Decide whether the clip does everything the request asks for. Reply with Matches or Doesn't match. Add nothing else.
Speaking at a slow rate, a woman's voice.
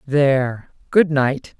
Matches